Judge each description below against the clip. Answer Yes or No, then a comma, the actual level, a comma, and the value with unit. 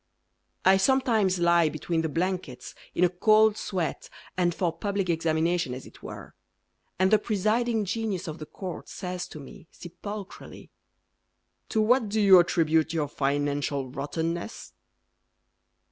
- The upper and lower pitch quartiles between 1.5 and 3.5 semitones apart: No, average, 4.3 semitones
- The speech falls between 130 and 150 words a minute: Yes, slow, 135 wpm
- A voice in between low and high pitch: Yes, medium, 180 Hz